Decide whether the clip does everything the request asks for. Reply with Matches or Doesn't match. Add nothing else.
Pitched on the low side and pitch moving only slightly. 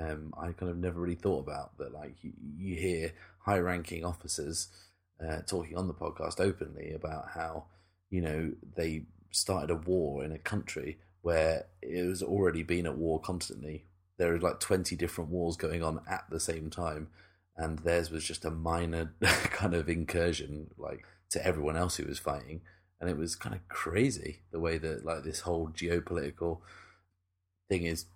Matches